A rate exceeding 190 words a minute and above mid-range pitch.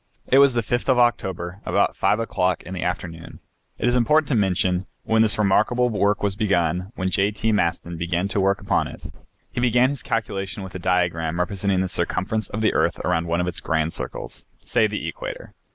No: fast, 205 wpm; low, 100 Hz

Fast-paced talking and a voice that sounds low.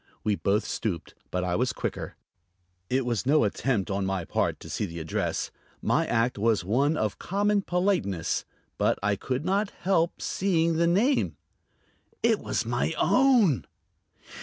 No: average, 155 wpm; low, 130 Hz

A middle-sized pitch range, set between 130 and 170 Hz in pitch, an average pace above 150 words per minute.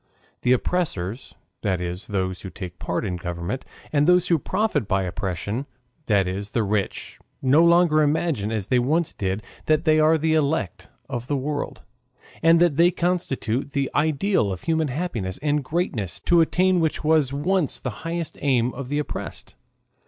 No: wide, 7.8 semitones; medium, 140 Hz; average, 170 wpm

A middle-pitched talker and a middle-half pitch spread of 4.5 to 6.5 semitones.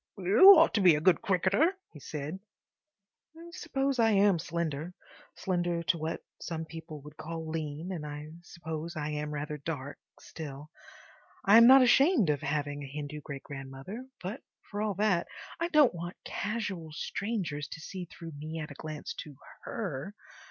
Yes: medium, 165 Hz; average, 5.1 semitones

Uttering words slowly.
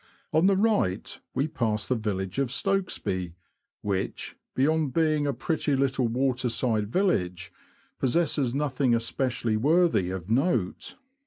Yes: slow, 125 wpm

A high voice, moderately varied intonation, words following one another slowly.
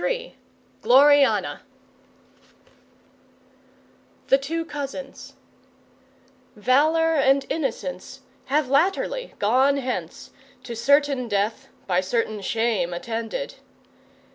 Yes: very high, 265 Hz; average, 4.3 semitones; slow, 75 wpm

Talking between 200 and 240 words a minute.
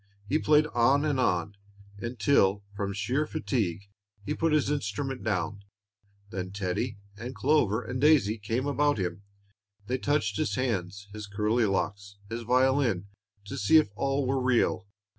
No: average, 150 wpm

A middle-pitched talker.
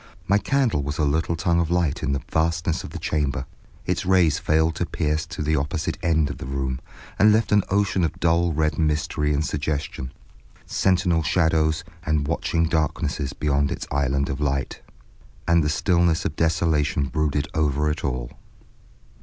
No: very low, 80 Hz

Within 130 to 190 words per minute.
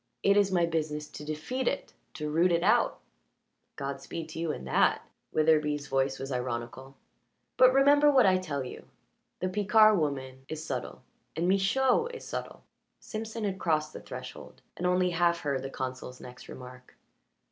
Yes: average, 165 wpm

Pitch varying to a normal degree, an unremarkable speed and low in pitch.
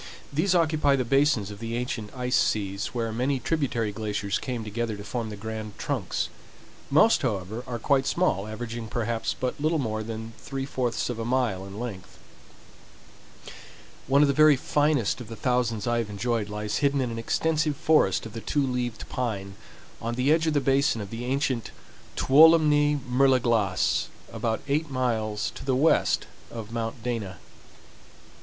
Yes: average, 3.9 semitones; average, 175 wpm; low, 120 Hz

